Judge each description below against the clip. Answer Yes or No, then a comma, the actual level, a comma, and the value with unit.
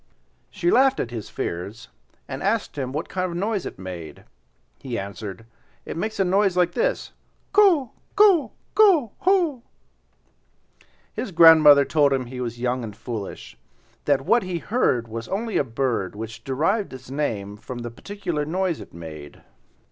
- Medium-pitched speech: Yes, medium, 145 Hz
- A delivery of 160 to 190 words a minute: Yes, average, 165 wpm